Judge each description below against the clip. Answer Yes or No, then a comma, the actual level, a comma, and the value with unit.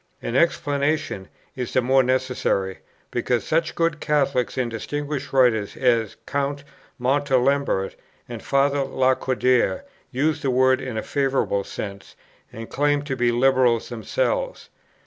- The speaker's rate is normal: No, slow, 125 wpm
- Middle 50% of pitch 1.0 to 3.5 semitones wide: Yes, average, 2.8 semitones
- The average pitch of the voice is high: No, low, 130 Hz